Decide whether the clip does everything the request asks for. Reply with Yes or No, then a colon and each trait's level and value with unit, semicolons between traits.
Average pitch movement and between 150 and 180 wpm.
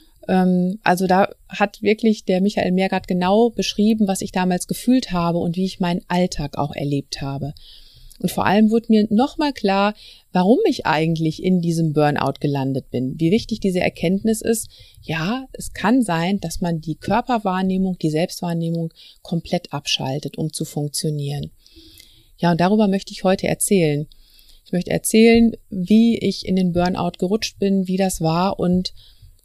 Yes: average, 4.2 semitones; average, 160 wpm